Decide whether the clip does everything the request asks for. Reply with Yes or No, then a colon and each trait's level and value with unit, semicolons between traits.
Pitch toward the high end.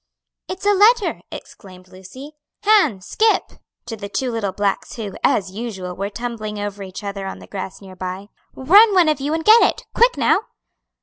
Yes: high, 215 Hz